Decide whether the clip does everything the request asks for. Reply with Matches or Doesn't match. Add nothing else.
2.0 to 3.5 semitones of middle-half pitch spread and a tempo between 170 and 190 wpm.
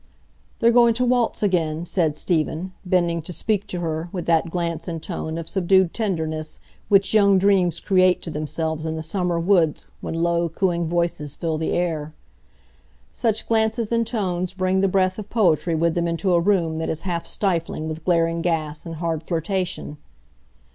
Matches